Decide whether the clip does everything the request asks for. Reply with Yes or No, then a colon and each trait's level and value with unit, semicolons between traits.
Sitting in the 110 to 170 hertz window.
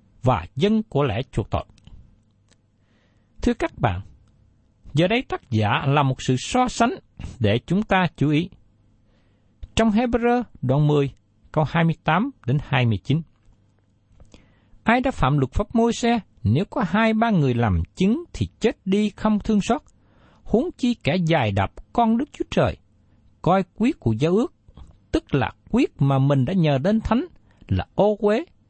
Yes: medium, 140 Hz